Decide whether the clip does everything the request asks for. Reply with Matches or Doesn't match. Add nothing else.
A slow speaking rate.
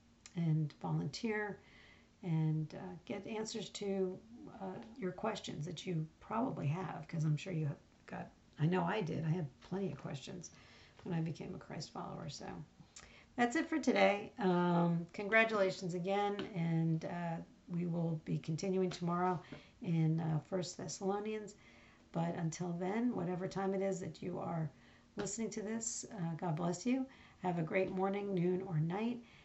Doesn't match